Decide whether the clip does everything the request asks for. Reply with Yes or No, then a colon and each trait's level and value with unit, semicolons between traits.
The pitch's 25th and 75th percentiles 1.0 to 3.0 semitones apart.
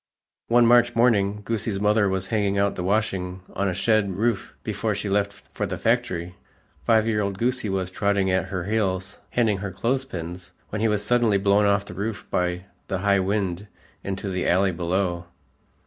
Yes: narrow, 2.5 semitones